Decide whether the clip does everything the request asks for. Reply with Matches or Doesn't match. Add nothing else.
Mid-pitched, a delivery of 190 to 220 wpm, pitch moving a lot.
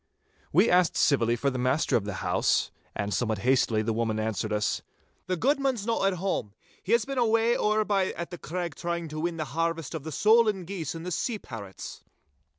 Matches